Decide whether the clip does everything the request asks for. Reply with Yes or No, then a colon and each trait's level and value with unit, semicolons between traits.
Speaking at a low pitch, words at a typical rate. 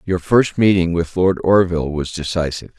Yes: very low, 90 Hz; average, 170 wpm